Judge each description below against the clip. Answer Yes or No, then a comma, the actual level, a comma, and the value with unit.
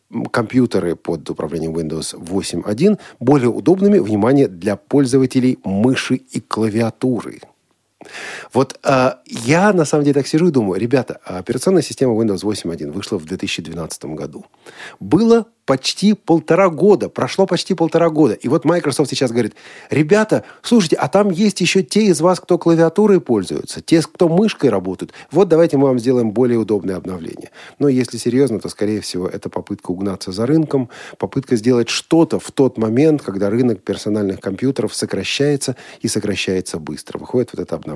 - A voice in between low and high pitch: No, low, 130 Hz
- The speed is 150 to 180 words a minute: Yes, average, 155 wpm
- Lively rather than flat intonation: Yes, wide, 7.7 semitones